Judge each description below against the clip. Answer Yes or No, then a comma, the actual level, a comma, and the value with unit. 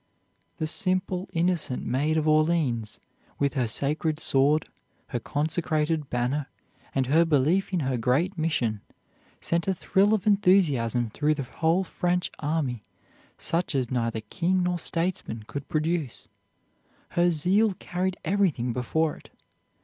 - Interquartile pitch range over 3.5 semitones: Yes, average, 5.1 semitones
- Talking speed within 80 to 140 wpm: Yes, slow, 135 wpm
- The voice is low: No, medium, 155 Hz